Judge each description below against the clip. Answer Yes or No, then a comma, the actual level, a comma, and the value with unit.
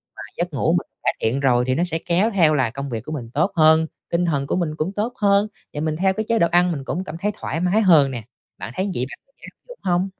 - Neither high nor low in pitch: Yes, medium, 165 Hz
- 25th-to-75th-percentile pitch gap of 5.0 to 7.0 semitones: Yes, average, 5.3 semitones